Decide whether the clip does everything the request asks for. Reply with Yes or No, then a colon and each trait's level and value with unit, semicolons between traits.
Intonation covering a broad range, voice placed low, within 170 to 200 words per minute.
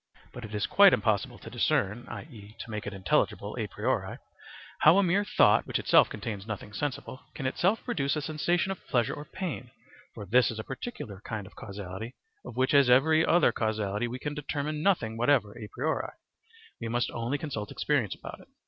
Yes: wide, 6.1 semitones; low, 120 Hz; average, 195 wpm